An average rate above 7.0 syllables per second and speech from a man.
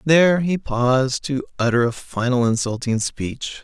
No: 4.5 syllables/s; male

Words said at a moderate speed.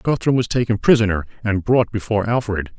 Yes: average, 170 wpm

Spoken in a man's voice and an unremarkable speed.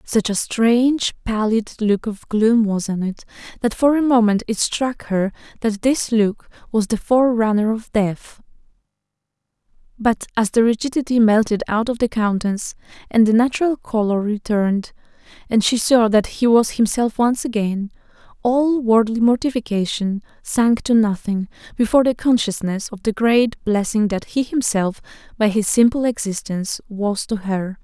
No: female; average, 155 wpm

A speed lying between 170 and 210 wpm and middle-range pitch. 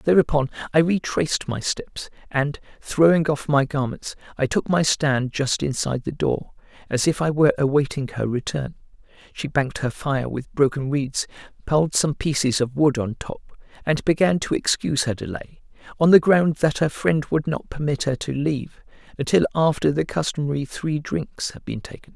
Yes: average, 180 wpm; medium, 145 Hz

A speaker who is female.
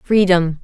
Yes: female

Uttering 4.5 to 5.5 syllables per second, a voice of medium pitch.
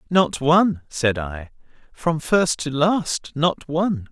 No: 3.5 syllables/s; medium, 150 Hz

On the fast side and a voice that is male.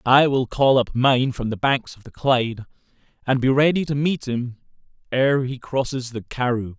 No: average, 195 wpm; male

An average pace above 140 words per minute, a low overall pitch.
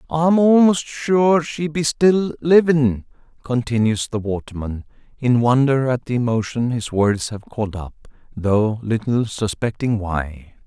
No: slow, 135 wpm; low, 125 Hz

